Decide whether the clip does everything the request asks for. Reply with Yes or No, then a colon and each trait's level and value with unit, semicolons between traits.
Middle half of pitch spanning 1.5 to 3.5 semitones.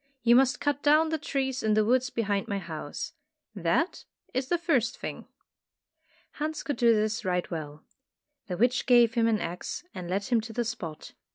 No: average, 5.0 semitones